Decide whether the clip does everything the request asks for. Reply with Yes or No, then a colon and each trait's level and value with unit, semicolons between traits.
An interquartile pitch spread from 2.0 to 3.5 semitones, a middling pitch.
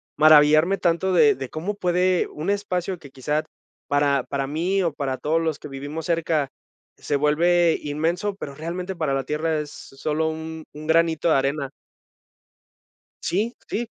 Yes: average, 3.1 semitones; medium, 160 Hz